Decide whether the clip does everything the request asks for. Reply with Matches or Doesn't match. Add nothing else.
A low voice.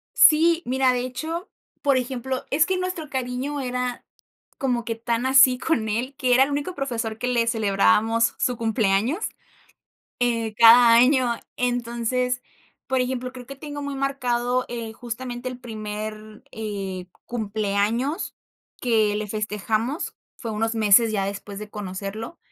Doesn't match